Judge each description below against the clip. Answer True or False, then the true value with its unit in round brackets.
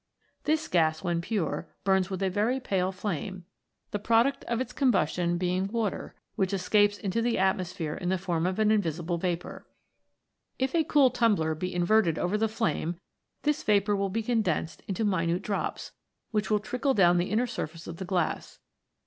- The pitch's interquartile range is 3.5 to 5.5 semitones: True (3.9 semitones)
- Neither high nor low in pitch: False (195 Hz)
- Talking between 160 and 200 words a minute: True (180 wpm)